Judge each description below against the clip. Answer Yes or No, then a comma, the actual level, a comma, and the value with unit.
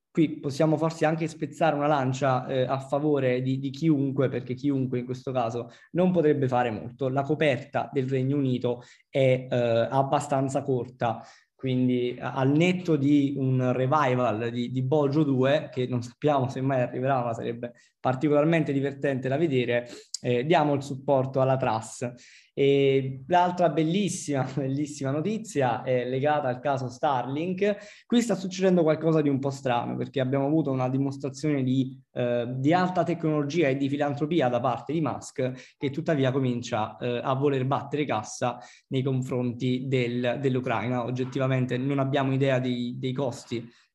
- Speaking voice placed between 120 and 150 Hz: Yes, low, 135 Hz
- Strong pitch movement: No, average, 2.9 semitones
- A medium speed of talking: Yes, average, 155 wpm